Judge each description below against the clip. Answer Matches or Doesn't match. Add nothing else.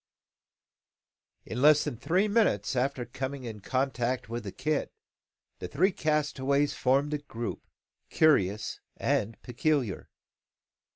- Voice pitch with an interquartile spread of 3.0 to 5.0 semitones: Matches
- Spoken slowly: Matches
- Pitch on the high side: Doesn't match